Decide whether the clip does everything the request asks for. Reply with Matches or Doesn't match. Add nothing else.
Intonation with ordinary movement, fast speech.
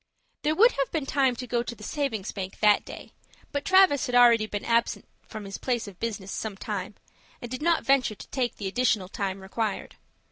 Matches